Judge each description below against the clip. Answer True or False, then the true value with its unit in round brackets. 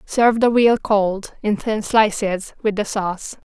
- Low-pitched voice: False (210 Hz)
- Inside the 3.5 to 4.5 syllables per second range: True (4.1 syllables/s)